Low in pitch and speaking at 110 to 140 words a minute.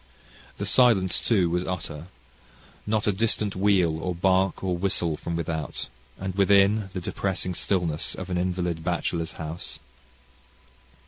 Yes: very low, 90 Hz; slow, 135 wpm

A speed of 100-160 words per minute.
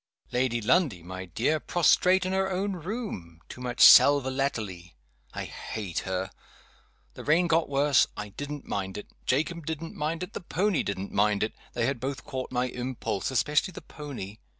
No: average, 175 wpm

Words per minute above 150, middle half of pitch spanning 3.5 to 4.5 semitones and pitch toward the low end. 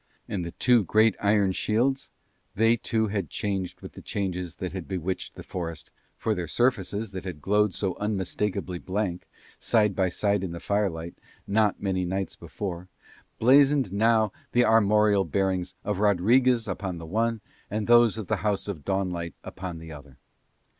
No: average, 165 wpm; average, 3.1 semitones; low, 100 Hz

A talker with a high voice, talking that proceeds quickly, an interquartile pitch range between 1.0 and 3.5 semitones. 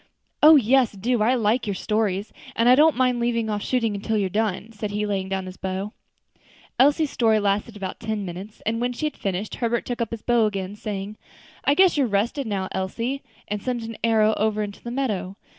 Yes: high, 220 Hz; fast, 210 wpm; average, 3.1 semitones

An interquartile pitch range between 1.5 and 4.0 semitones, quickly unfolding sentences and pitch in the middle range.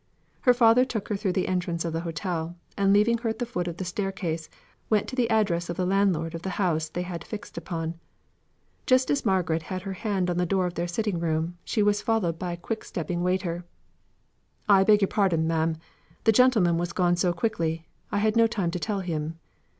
Yes: average, 3.7 semitones; fast, 220 wpm; medium, 180 Hz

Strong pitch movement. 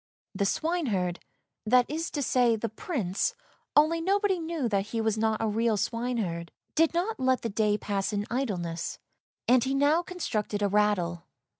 Yes: wide, 6.3 semitones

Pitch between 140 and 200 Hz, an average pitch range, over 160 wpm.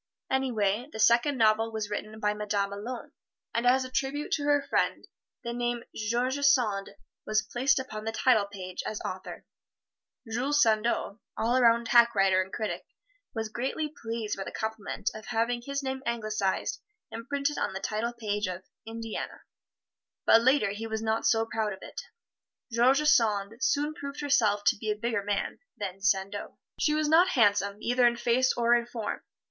No: high, 230 Hz; average, 3.3 semitones; average, 175 wpm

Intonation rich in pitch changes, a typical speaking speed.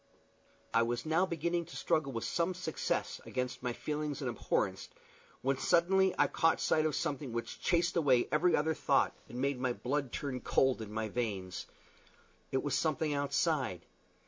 No: average, 4.7 semitones; average, 170 wpm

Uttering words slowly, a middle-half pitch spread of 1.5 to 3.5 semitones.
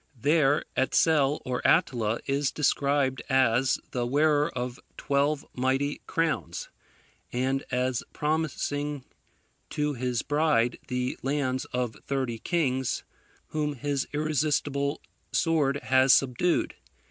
Yes: slow, 105 wpm; narrow, 2.6 semitones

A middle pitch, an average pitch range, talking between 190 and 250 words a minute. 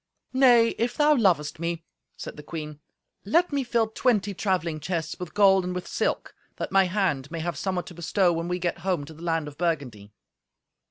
Yes: medium, 180 Hz; average, 4.0 semitones; average, 200 wpm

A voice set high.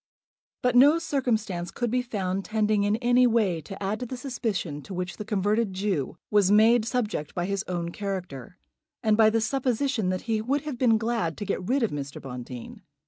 Yes: high, 215 Hz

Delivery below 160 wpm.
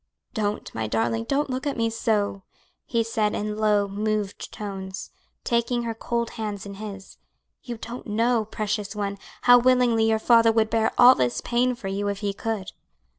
No: average, 175 wpm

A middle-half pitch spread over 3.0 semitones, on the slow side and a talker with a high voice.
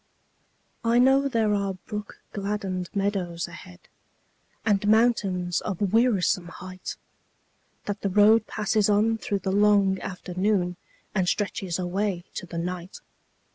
No: narrow, 2.5 semitones; slow, 125 wpm; high, 200 Hz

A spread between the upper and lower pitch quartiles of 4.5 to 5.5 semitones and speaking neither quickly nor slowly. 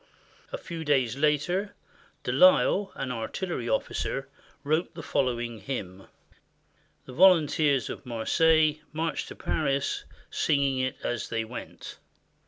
No: average, 4.8 semitones; slow, 120 wpm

